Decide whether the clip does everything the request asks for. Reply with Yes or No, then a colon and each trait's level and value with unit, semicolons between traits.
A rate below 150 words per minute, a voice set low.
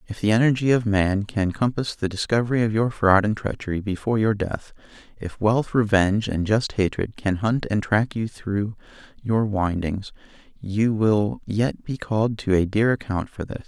No: average, 185 wpm; low, 105 Hz